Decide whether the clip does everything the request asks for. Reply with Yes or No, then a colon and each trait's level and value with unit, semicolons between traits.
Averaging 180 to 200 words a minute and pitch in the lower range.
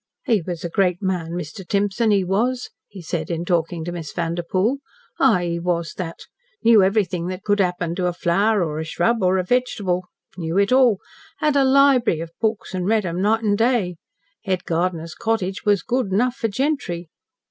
No: average, 190 wpm; medium, 185 Hz